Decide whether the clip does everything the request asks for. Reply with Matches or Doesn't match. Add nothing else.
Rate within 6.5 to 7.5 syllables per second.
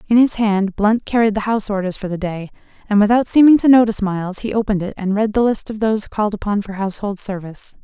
Matches